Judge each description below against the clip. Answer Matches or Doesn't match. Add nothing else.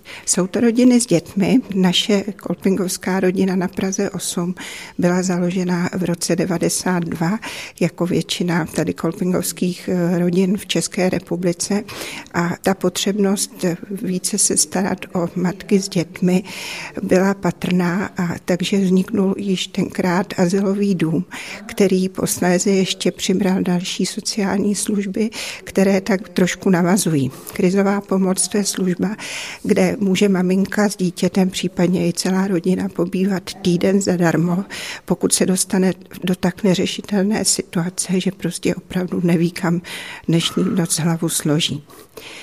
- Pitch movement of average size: Doesn't match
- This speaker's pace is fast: Doesn't match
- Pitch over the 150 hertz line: Matches